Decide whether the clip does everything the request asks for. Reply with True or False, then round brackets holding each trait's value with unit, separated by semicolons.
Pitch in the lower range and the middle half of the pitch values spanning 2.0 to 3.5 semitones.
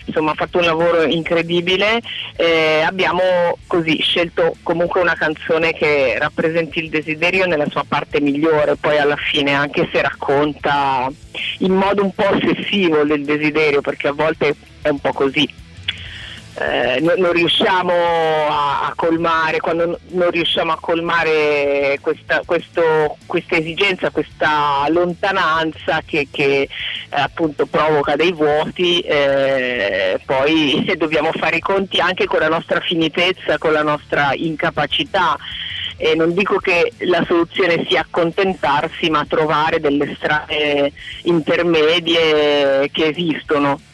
False (160 Hz; 2.8 semitones)